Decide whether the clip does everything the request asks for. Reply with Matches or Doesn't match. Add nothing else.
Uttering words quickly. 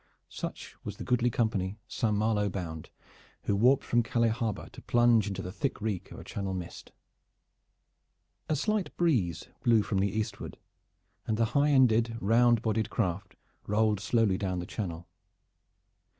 Doesn't match